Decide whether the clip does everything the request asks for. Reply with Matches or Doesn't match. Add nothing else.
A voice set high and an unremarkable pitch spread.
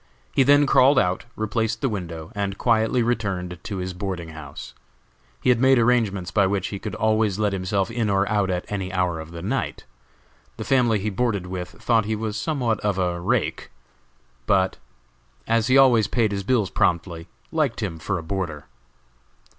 Doesn't match